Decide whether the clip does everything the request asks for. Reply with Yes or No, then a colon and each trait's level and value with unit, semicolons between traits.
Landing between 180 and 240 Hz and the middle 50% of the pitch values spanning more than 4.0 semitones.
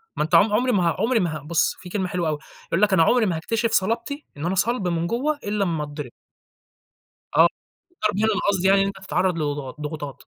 Yes: medium, 185 Hz; average, 4.7 semitones